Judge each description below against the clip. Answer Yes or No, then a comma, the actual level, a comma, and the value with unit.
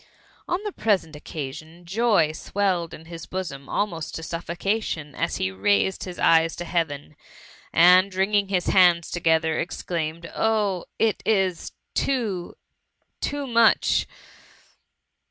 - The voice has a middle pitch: Yes, medium, 175 Hz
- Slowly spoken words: Yes, slow, 130 wpm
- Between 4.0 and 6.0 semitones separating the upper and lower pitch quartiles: No, average, 3.6 semitones